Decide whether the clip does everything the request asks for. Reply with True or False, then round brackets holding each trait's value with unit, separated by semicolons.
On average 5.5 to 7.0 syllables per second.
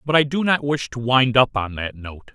False (4.9 syllables/s)